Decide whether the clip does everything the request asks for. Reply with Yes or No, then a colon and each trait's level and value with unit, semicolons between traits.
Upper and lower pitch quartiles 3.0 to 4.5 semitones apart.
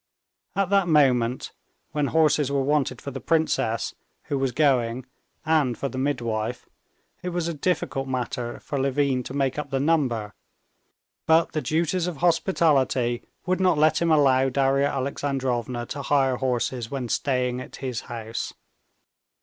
Yes: average, 3.4 semitones